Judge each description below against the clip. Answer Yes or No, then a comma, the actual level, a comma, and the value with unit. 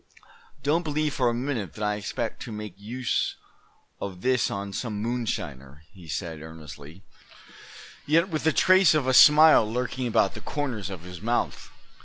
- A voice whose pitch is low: Yes, low, 110 Hz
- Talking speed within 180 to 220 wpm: No, average, 165 wpm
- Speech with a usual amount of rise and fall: No, wide, 6.5 semitones